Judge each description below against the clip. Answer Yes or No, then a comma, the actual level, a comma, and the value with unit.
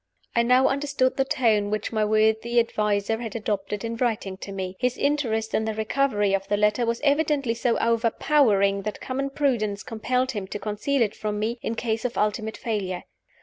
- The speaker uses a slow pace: No, average, 190 wpm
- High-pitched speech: Yes, high, 225 Hz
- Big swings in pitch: No, average, 3.2 semitones